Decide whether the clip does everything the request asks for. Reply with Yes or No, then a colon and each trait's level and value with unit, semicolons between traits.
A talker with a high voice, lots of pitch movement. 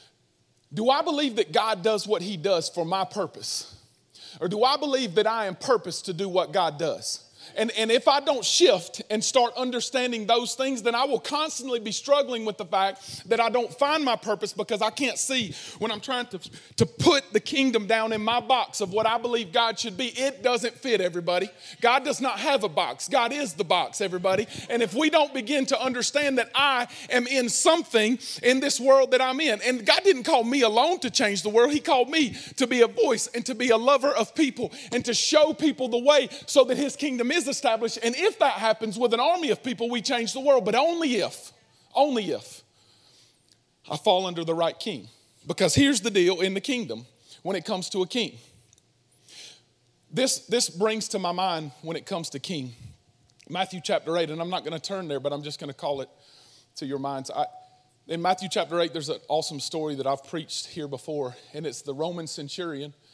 Yes: high, 225 Hz; wide, 6.1 semitones